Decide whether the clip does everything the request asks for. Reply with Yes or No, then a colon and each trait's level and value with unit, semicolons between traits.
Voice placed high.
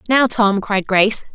Yes: high, 210 Hz